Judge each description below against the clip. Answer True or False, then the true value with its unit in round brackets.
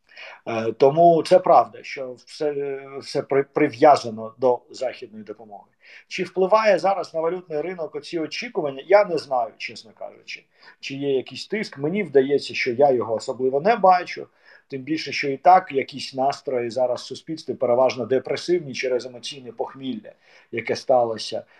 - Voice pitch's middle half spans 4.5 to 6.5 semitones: True (4.8 semitones)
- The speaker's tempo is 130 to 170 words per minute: True (140 wpm)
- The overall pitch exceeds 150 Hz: False (140 Hz)